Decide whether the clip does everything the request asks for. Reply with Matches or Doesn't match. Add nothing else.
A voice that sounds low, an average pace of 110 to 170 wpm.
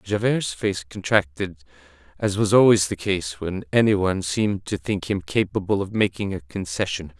Matches